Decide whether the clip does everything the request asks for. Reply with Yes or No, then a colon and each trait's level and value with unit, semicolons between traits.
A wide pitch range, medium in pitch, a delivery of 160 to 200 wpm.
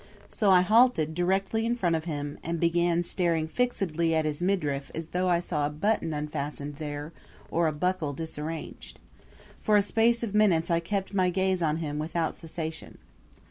No: average, 3.5 semitones; medium, 170 Hz; average, 180 wpm